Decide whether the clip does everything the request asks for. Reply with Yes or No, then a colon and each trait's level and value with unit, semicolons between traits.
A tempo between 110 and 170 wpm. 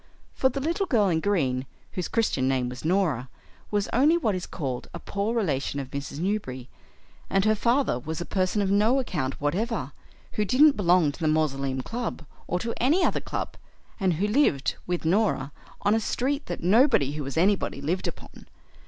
No: average, 190 wpm